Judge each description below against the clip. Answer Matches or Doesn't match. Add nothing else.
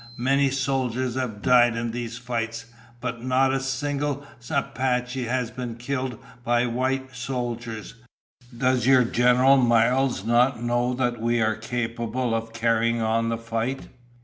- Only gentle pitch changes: Matches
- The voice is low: Matches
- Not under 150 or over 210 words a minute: Doesn't match